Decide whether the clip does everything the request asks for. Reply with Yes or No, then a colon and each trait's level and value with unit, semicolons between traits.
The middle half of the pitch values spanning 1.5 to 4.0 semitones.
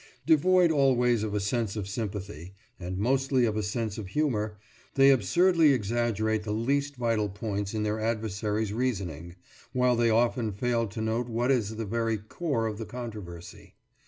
Yes: average, 2.9 semitones